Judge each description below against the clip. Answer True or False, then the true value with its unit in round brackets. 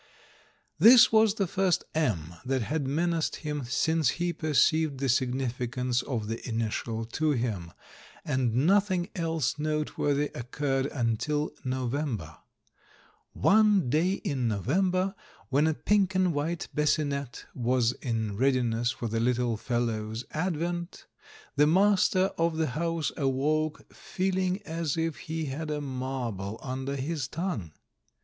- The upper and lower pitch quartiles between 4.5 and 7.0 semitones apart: True (5.2 semitones)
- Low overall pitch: False (145 Hz)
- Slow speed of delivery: True (125 wpm)